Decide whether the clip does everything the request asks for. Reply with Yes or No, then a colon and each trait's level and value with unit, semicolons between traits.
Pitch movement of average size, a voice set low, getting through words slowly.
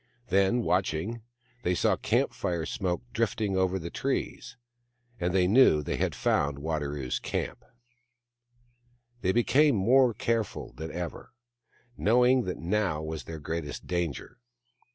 No: wide, 6.1 semitones; very low, 90 Hz; slow, 130 wpm